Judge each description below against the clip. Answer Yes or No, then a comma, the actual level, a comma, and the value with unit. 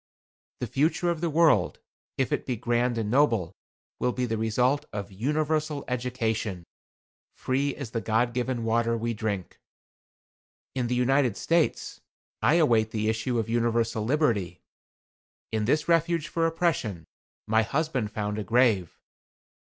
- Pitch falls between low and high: No, low, 120 Hz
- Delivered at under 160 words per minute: Yes, average, 145 wpm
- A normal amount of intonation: Yes, average, 4.5 semitones